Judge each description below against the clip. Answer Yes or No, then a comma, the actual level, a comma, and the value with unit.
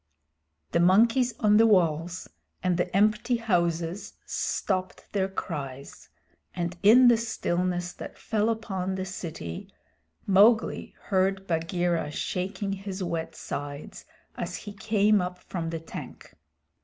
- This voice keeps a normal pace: No, slow, 125 wpm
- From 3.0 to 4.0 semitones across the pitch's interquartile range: Yes, average, 3.5 semitones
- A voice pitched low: No, medium, 185 Hz